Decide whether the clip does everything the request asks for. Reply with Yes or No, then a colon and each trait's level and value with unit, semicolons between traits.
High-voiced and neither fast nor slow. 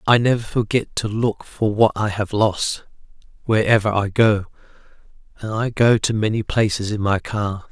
No: low, 105 Hz; average, 170 wpm